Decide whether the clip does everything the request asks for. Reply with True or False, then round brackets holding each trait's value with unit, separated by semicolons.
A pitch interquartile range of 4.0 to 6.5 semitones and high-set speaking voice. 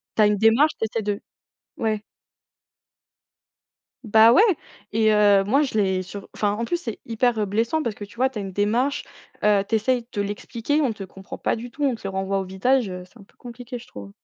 False (3.3 semitones; 220 Hz)